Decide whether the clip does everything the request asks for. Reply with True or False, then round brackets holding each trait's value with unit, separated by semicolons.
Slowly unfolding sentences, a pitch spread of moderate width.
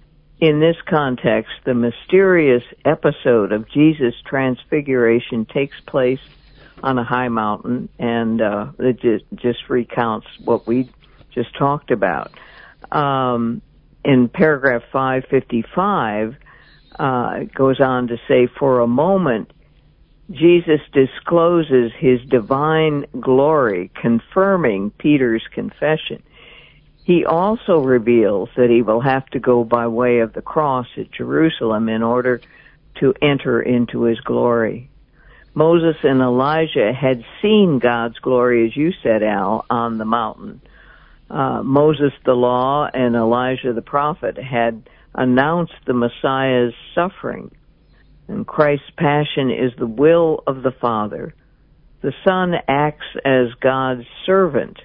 True (125 wpm; 4.0 semitones)